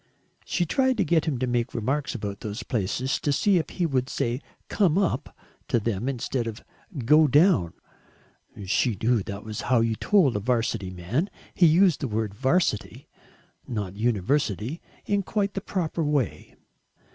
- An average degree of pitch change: No, wide, 7.0 semitones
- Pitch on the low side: Yes, low, 130 Hz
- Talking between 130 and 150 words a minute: No, average, 165 wpm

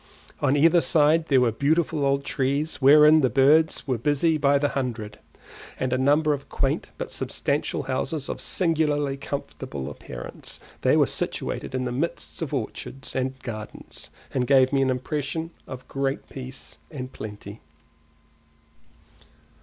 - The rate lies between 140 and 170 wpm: Yes, average, 145 wpm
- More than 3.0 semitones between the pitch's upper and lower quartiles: No, average, 2.7 semitones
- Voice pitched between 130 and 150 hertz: Yes, medium, 140 Hz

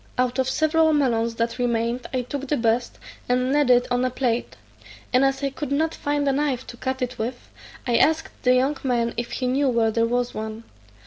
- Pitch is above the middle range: Yes, very high, 255 Hz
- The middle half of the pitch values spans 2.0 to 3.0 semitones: Yes, narrow, 2.6 semitones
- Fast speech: Yes, fast, 215 wpm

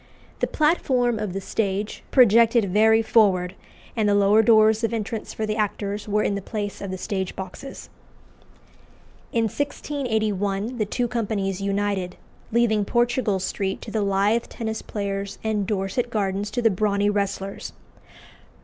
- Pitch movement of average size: No, narrow, 2.2 semitones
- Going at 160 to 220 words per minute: No, average, 150 wpm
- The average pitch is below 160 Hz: No, high, 210 Hz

